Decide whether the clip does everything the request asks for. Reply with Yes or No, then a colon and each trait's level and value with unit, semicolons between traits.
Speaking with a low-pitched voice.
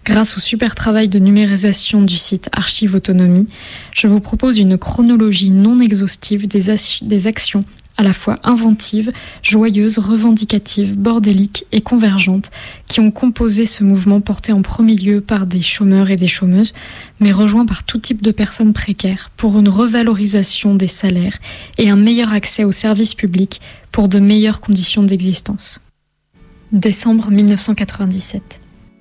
No: high, 210 Hz